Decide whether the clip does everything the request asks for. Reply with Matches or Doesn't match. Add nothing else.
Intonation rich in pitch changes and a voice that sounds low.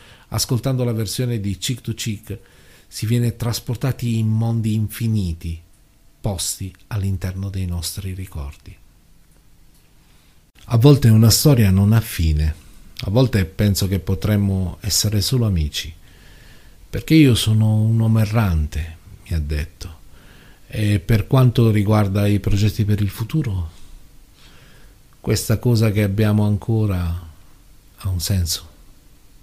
Doesn't match